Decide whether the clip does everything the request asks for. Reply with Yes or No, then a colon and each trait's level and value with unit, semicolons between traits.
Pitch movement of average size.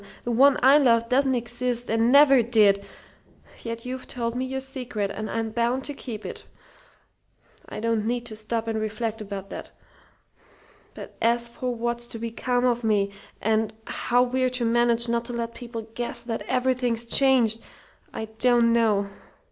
No: narrow, 1.8 semitones